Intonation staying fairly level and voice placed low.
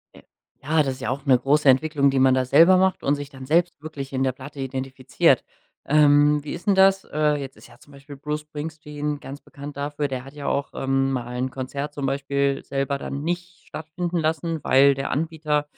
No: narrow, 2.1 semitones; medium, 145 Hz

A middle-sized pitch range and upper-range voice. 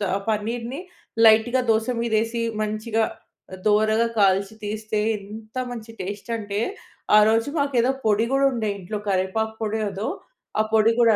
No: narrow, 1.7 semitones; high, 220 Hz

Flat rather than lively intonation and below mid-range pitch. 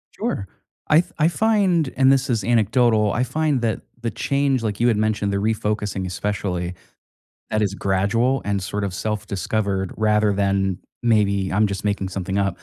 No: average, 3.4 semitones; low, 105 Hz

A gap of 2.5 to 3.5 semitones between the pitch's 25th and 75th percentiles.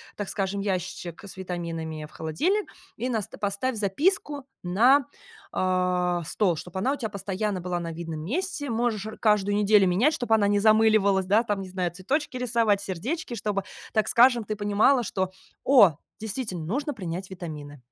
No: average, 4.2 semitones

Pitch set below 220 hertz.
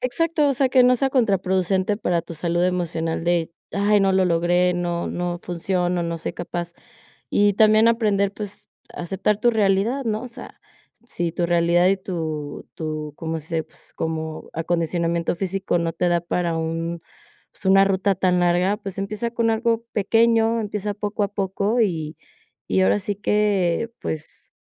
Yes: medium, 185 Hz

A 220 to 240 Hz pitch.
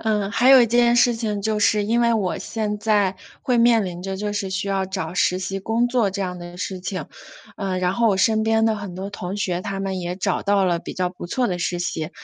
No: high, 200 Hz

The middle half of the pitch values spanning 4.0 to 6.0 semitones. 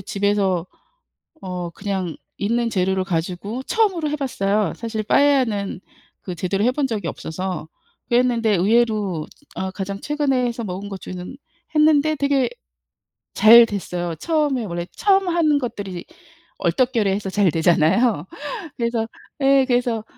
Yes: wide, 5.4 semitones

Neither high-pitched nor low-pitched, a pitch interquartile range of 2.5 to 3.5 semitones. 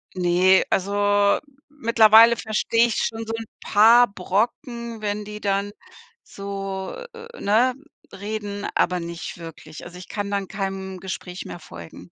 No: high, 205 Hz; average, 2.8 semitones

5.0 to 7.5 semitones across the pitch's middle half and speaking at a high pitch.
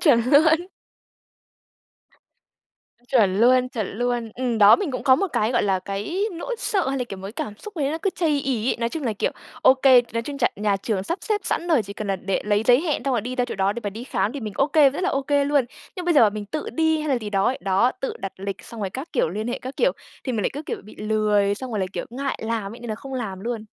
Yes: average, 5.3 semitones; high, 245 Hz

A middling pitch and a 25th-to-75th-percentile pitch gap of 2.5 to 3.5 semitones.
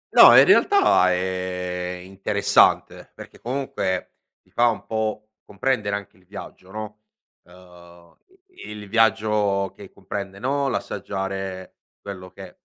No: low, 100 Hz; average, 2.8 semitones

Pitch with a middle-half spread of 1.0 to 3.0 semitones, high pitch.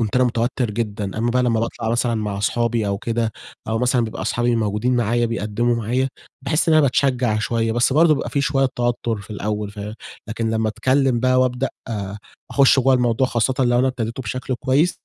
No: narrow, 2.5 semitones; low, 120 Hz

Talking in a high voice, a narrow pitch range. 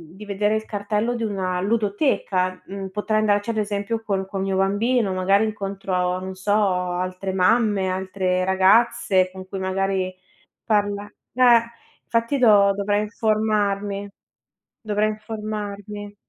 Yes: high, 205 Hz; narrow, 2.2 semitones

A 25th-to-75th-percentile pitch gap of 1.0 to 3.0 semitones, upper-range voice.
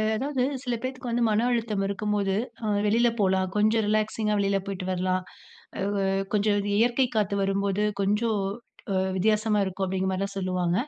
Yes: narrow, 2.4 semitones; high, 205 Hz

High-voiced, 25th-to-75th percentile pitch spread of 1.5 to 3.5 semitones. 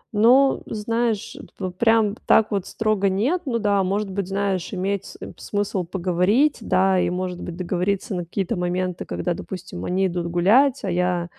Yes: high, 195 Hz; average, 2.9 semitones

